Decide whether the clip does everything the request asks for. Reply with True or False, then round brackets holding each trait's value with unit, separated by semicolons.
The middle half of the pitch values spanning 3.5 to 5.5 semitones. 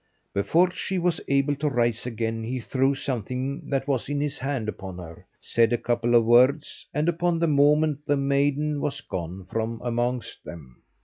True (4.0 semitones)